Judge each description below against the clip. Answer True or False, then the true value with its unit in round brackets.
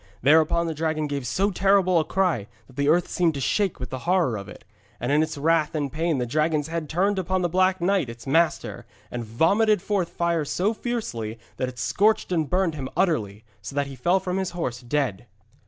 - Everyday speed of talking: False (215 wpm)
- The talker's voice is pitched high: False (160 Hz)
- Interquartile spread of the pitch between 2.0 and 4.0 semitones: False (5.1 semitones)